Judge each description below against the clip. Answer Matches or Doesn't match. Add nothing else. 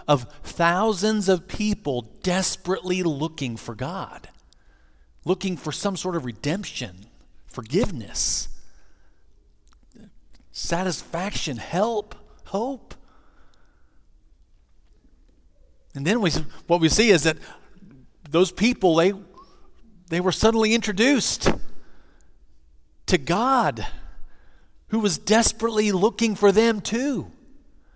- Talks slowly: Matches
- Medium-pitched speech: Matches